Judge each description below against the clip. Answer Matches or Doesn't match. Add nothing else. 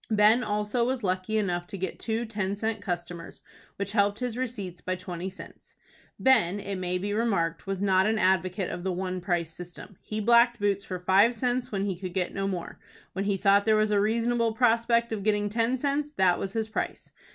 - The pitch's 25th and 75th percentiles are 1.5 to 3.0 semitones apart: Doesn't match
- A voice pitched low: Doesn't match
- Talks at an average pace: Doesn't match